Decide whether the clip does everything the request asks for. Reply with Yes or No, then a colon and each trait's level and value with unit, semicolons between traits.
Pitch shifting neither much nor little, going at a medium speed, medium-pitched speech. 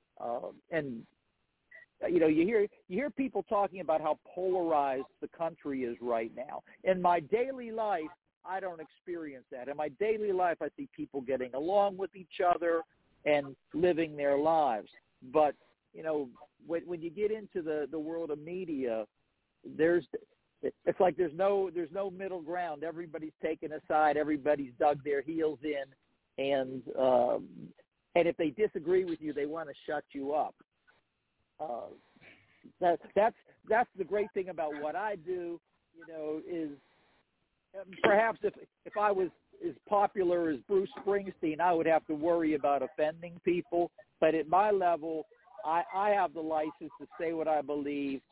Yes: average, 4.1 semitones; average, 165 wpm; medium, 170 Hz